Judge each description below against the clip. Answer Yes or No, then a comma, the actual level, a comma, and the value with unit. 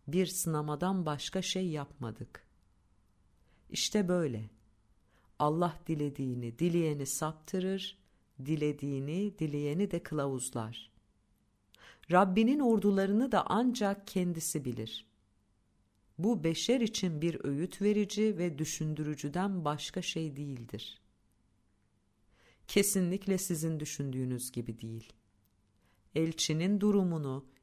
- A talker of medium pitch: Yes, medium, 150 Hz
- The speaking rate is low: Yes, slow, 85 wpm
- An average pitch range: No, wide, 8.8 semitones